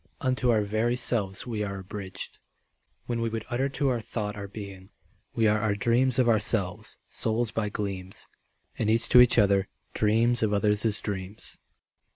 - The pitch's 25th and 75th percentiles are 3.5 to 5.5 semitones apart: No, narrow, 2.6 semitones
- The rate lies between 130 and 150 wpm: No, average, 170 wpm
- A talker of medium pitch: No, low, 110 Hz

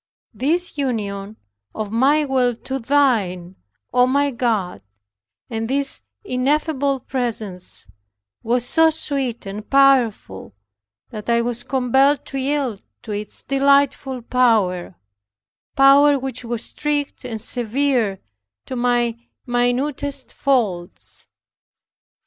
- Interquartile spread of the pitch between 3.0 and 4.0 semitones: Yes, average, 3.7 semitones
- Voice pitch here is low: No, very high, 250 Hz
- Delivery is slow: Yes, slow, 105 wpm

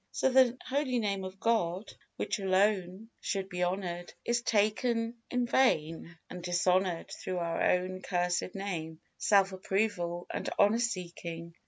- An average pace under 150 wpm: Yes, average, 140 wpm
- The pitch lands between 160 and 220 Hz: Yes, high, 190 Hz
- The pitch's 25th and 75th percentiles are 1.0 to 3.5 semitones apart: No, average, 4.0 semitones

